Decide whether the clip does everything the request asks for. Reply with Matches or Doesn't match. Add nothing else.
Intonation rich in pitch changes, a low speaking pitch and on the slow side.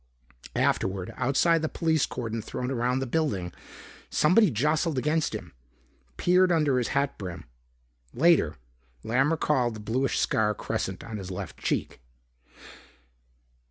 Matches